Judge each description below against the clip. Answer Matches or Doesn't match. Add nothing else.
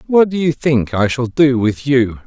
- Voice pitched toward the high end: Doesn't match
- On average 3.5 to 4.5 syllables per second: Matches